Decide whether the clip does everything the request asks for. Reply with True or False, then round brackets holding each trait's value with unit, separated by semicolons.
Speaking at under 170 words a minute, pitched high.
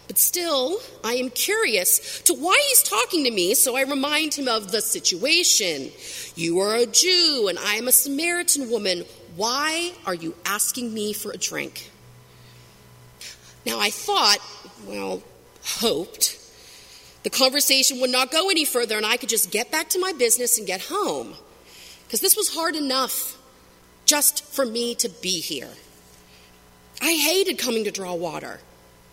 True (160 wpm; 245 Hz)